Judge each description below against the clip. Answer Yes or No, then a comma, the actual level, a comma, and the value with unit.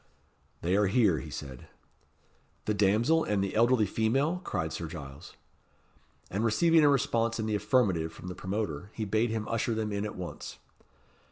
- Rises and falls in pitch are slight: No, average, 4.0 semitones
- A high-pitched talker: No, low, 105 Hz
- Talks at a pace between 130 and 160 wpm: No, average, 170 wpm